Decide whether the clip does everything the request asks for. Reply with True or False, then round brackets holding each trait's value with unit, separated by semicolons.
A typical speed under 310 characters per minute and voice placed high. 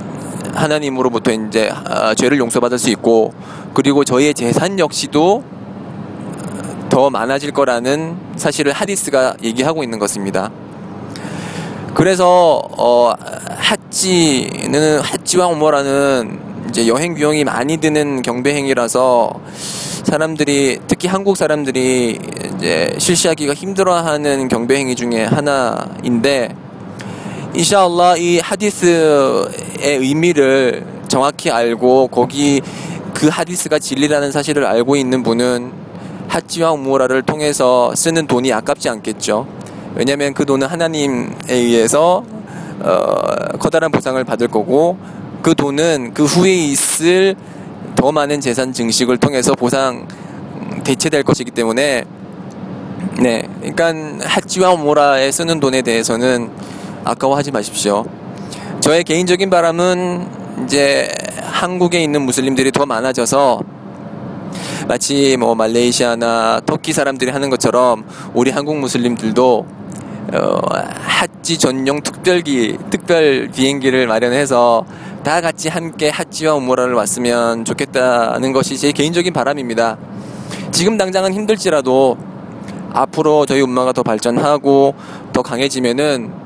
False (275 characters per minute; 140 Hz)